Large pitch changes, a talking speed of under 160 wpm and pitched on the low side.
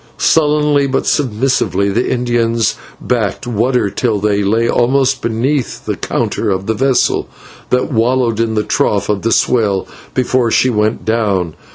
No: average, 3.4 semitones; average, 150 wpm; low, 115 Hz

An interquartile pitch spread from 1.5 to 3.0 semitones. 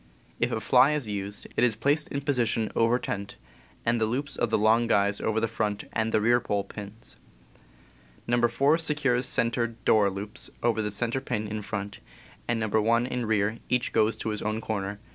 Yes: narrow, 2.5 semitones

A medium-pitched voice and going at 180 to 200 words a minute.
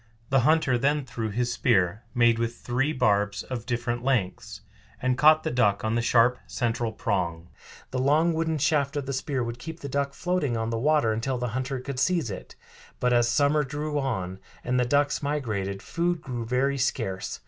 No: low, 125 Hz; average, 190 wpm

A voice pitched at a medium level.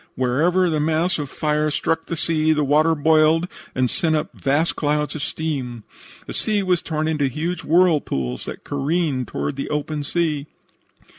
Yes: medium, 155 Hz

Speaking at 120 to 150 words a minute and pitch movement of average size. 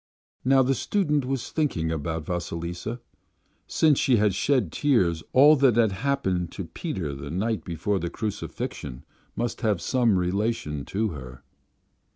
No: average, 145 wpm; wide, 7.3 semitones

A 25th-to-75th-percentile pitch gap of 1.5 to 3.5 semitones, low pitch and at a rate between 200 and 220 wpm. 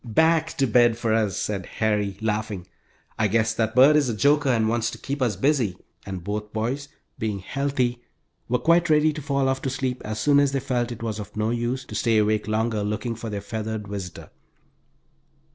No: average, 3.9 semitones; low, 115 Hz; fast, 205 wpm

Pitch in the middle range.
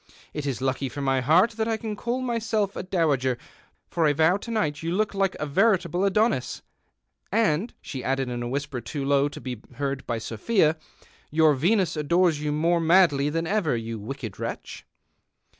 Yes: medium, 155 Hz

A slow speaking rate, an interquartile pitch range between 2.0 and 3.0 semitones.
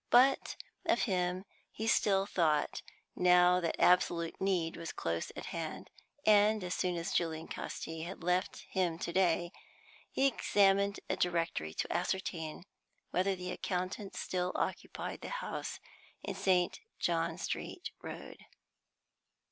Yes: slow, 130 wpm; narrow, 2.4 semitones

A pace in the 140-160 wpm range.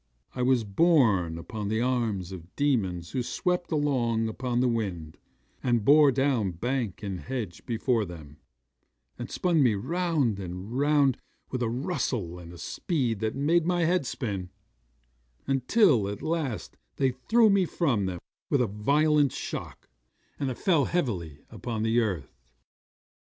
Yes: average, 150 wpm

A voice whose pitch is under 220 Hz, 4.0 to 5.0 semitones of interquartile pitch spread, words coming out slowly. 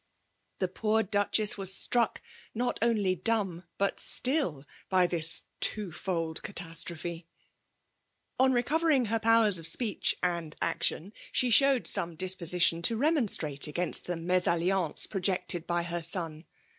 Yes: medium, 185 Hz; average, 4.7 semitones; slow, 130 wpm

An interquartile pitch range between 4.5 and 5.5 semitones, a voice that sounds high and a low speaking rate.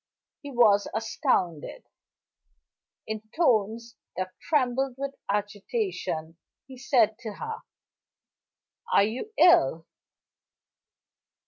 Yes: average, 5.2 semitones; high, 230 Hz; slow, 85 wpm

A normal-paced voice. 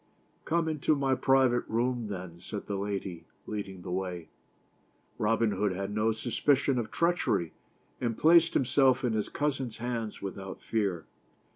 Yes: average, 150 wpm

